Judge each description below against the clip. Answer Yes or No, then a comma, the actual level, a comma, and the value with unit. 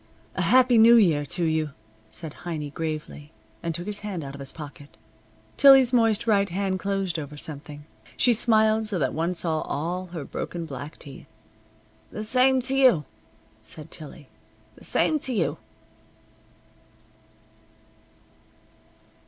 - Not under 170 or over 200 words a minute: No, average, 140 wpm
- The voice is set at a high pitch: No, medium, 175 Hz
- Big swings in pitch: Yes, wide, 6.4 semitones